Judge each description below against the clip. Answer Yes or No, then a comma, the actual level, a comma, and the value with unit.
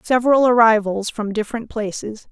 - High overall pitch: Yes, high, 220 Hz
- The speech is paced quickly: No, slow, 130 wpm